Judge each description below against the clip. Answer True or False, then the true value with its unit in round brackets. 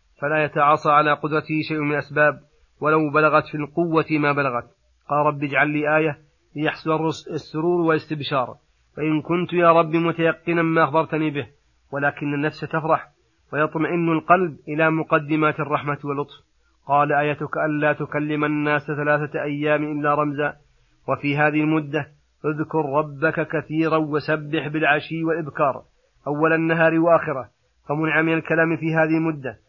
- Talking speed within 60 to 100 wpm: False (130 wpm)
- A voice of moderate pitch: True (155 Hz)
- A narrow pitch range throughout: True (1.5 semitones)